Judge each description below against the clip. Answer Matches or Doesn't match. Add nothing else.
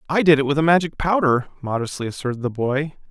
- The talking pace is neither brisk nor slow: Doesn't match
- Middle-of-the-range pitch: Matches